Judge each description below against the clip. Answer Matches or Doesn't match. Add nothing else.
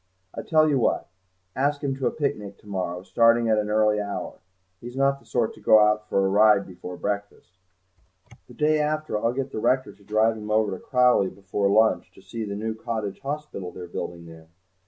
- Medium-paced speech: Doesn't match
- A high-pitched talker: Doesn't match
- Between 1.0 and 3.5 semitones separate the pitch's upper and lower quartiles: Doesn't match